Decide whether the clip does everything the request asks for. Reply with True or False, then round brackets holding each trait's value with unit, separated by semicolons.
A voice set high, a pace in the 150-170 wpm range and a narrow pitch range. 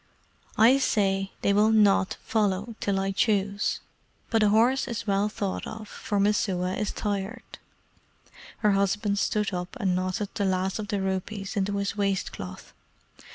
True (200 Hz; 155 wpm; 1.7 semitones)